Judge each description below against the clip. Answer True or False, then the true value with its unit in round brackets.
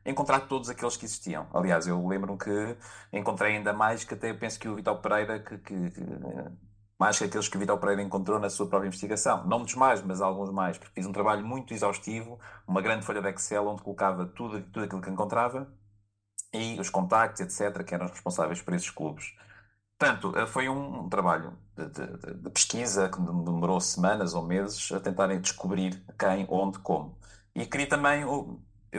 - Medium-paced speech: False (190 wpm)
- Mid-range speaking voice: False (100 Hz)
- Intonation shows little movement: True (2.2 semitones)